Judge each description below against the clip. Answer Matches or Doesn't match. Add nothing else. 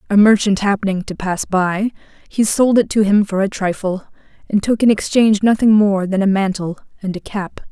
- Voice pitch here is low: Doesn't match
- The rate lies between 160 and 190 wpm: Doesn't match